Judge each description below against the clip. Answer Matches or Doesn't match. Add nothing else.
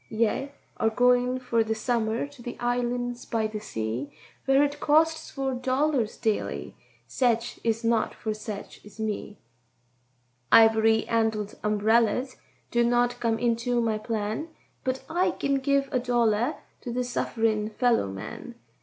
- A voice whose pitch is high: Matches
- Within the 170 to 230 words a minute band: Doesn't match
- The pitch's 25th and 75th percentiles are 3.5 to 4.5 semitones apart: Doesn't match